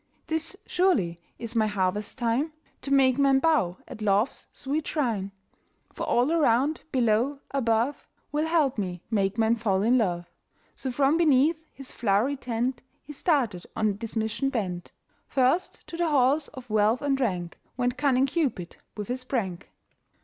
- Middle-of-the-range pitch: No, very high, 250 Hz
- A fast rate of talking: No, average, 155 wpm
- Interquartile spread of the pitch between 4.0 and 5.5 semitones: Yes, average, 4.8 semitones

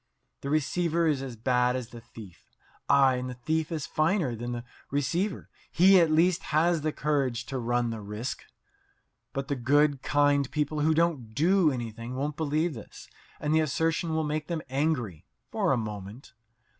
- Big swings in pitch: No, average, 4.4 semitones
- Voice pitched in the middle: Yes, medium, 145 Hz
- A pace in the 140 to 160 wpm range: No, average, 175 wpm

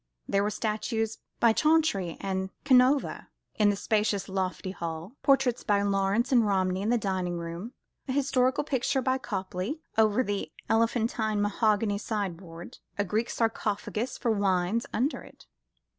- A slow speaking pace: No, average, 145 wpm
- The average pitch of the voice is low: No, high, 210 Hz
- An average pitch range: Yes, average, 3.8 semitones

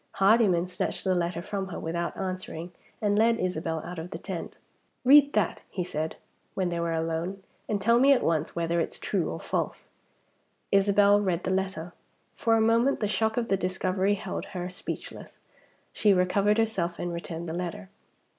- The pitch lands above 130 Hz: Yes, medium, 185 Hz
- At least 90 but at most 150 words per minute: No, average, 180 wpm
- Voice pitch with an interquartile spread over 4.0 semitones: No, average, 3.3 semitones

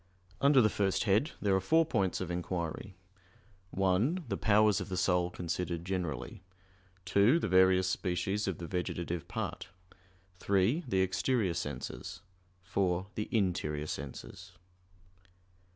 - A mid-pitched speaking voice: No, very low, 95 Hz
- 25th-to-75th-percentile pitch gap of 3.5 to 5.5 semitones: No, narrow, 2.5 semitones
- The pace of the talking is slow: Yes, slow, 130 wpm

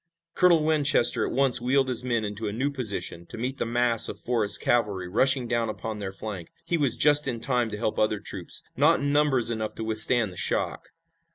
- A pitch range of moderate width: Yes, average, 3.9 semitones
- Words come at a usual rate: No, fast, 210 wpm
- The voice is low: Yes, low, 120 Hz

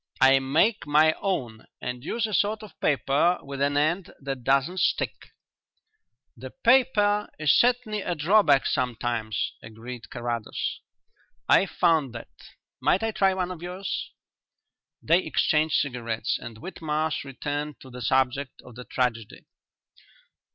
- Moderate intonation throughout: No, wide, 6.5 semitones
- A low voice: No, medium, 145 Hz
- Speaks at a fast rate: No, slow, 135 wpm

